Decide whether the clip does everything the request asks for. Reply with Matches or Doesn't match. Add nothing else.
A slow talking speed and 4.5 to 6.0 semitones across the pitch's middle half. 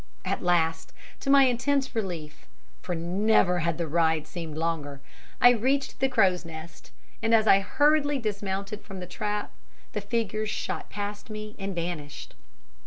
Doesn't match